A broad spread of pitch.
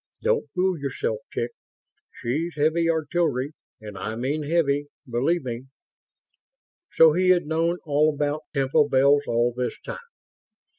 No: average, 4.0 semitones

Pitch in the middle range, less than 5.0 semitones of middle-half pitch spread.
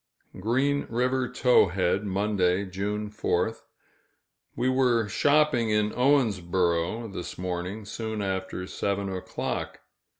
No: low, 105 Hz; average, 4.2 semitones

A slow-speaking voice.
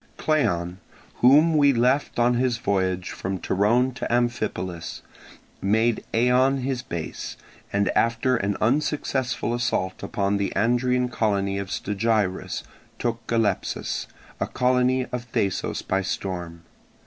Yes: slow, 120 wpm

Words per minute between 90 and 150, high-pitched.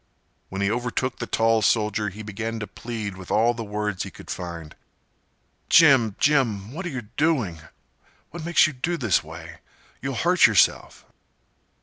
No: average, 140 wpm; low, 110 Hz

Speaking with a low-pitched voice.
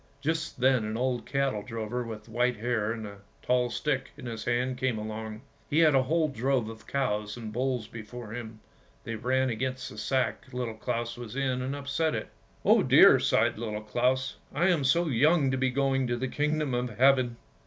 Yes: low, 125 Hz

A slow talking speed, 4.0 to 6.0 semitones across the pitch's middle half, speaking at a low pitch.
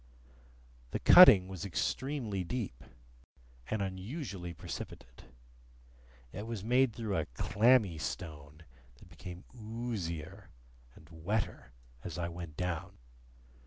Yes: slow, 105 wpm; average, 5.1 semitones; very low, 95 Hz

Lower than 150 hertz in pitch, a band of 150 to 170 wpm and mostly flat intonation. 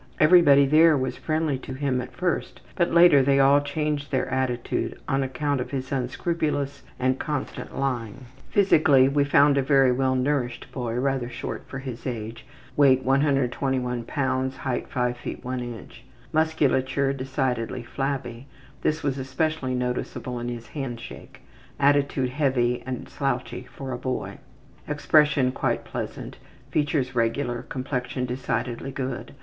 No: low, 135 Hz; average, 140 wpm; narrow, 2.2 semitones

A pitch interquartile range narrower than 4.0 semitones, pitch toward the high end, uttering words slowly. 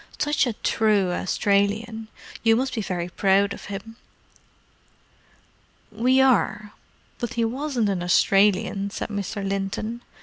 Yes: average, 2.8 semitones; high, 210 Hz; slow, 115 wpm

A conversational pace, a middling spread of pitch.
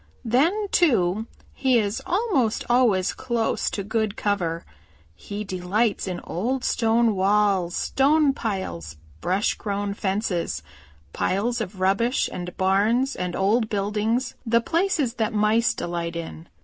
No: slow, 125 wpm; average, 4.1 semitones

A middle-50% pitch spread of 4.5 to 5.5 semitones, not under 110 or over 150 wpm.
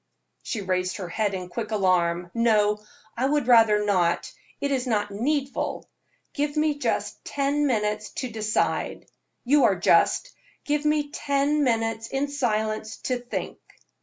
Yes: average, 5.2 semitones; average, 145 wpm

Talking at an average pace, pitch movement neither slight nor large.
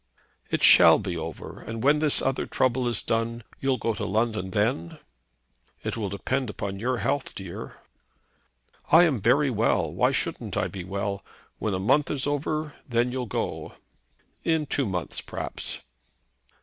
Yes: average, 160 wpm; average, 5.0 semitones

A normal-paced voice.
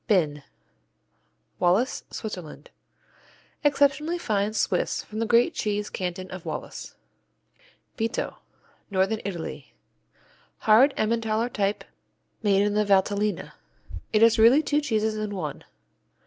No: slow, 110 wpm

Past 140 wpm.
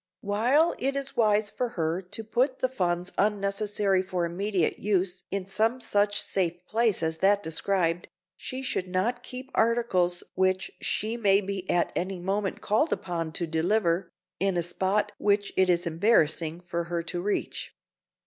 Yes: average, 160 wpm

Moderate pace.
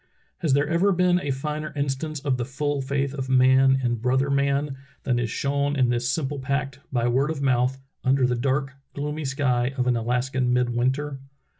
Yes: average, 185 wpm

